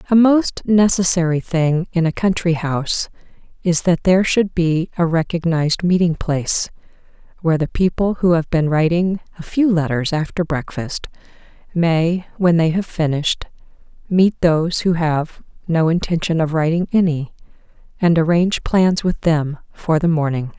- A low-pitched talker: No, medium, 170 Hz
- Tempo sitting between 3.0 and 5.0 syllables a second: Yes, 4.7 syllables/s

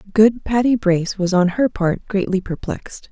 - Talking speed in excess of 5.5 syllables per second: No, 5.0 syllables/s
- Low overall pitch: No, high, 200 Hz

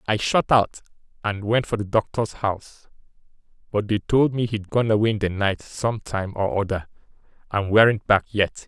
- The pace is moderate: Yes, average, 185 wpm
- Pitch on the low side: Yes, low, 105 Hz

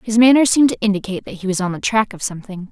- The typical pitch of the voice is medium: No, high, 210 Hz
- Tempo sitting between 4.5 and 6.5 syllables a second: No, 7.8 syllables/s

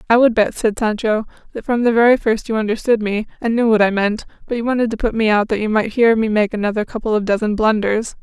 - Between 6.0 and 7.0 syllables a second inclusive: Yes, 6.2 syllables/s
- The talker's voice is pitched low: No, high, 220 Hz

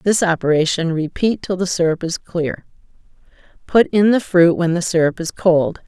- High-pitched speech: No, medium, 175 Hz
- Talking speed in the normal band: Yes, average, 165 wpm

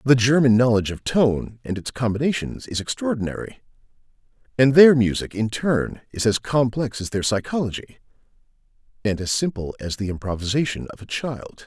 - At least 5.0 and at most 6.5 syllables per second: Yes, 5.3 syllables/s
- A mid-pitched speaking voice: No, low, 120 Hz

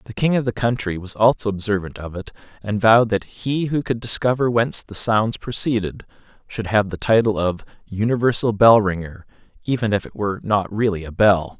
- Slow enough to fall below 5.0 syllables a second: No, 5.5 syllables/s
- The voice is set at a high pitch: No, low, 110 Hz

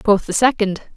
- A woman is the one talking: Yes, female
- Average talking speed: Yes, average, 190 wpm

